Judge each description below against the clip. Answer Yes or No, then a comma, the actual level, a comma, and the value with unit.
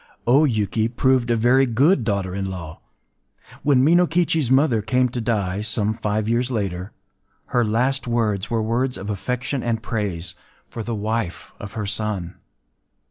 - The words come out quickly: No, average, 150 wpm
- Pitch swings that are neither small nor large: Yes, average, 3.5 semitones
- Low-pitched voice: Yes, low, 115 Hz